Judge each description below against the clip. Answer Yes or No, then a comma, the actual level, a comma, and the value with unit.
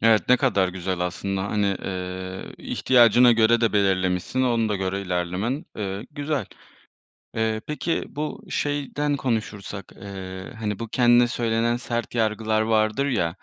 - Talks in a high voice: No, low, 110 Hz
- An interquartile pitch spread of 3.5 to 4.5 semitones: Yes, average, 3.9 semitones